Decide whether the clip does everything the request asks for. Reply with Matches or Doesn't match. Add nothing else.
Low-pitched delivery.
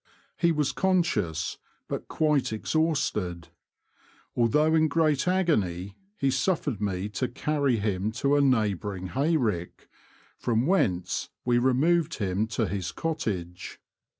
Matches